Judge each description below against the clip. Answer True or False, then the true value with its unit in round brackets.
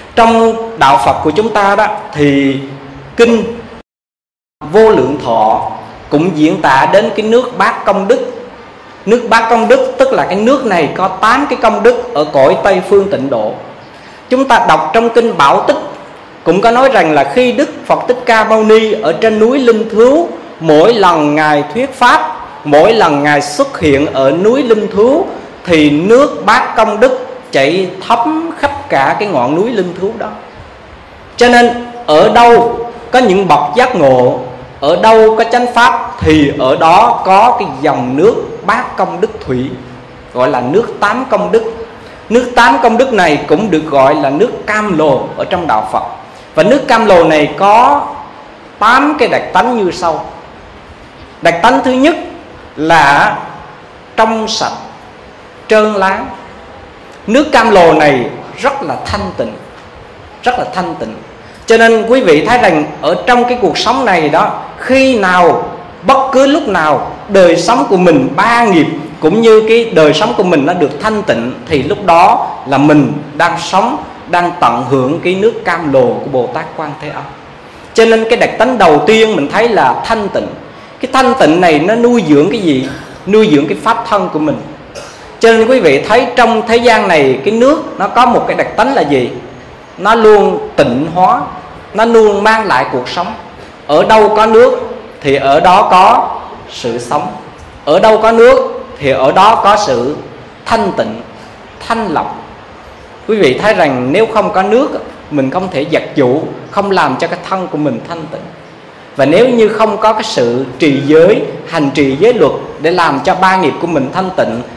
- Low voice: False (220 Hz)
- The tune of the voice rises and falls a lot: True (5.9 semitones)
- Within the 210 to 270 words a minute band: False (185 wpm)